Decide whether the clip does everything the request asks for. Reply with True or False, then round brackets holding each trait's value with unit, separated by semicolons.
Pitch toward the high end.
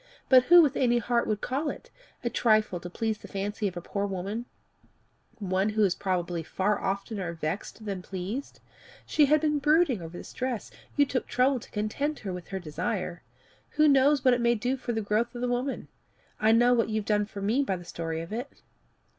True (215 Hz)